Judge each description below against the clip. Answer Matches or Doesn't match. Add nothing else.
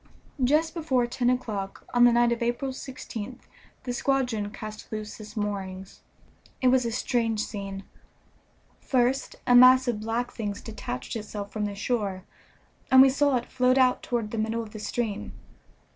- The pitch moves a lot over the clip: Doesn't match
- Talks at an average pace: Matches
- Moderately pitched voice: Doesn't match